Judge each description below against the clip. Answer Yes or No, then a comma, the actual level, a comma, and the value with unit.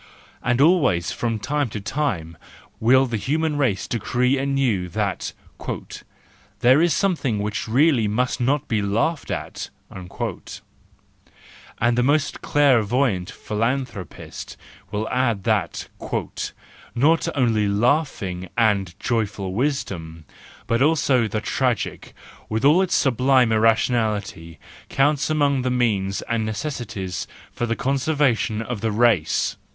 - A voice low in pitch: Yes, low, 120 Hz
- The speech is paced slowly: Yes, slow, 120 wpm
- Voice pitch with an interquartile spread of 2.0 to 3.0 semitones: No, average, 4.7 semitones